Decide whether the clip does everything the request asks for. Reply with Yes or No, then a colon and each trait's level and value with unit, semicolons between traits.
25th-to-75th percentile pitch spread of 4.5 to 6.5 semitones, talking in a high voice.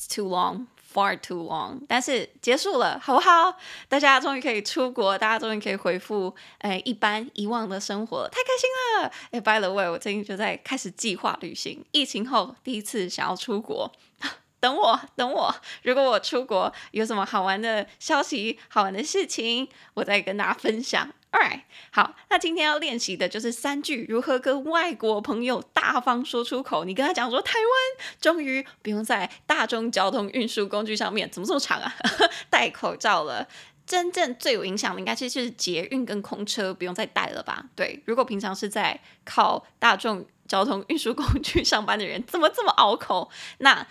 Yes: average, 4.9 semitones; high, 230 Hz